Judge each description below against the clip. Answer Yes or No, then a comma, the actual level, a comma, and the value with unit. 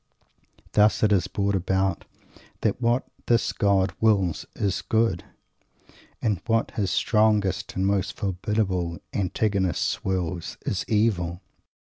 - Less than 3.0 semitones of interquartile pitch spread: Yes, narrow, 2.6 semitones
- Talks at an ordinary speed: No, slow, 115 wpm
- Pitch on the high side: No, low, 100 Hz